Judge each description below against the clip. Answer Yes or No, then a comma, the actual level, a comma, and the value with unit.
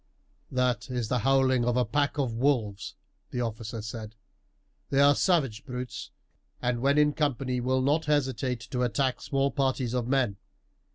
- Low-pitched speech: Yes, low, 125 Hz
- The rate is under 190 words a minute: Yes, average, 160 wpm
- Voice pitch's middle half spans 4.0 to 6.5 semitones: No, narrow, 2.5 semitones